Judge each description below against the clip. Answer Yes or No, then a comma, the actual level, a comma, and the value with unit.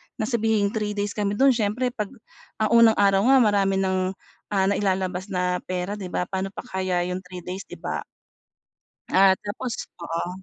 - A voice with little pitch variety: Yes, narrow, 2.3 semitones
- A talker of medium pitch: No, high, 195 Hz